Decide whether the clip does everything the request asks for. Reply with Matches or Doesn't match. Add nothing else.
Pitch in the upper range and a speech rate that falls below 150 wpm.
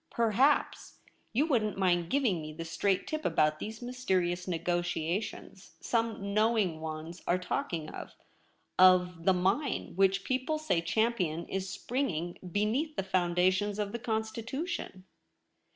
Matches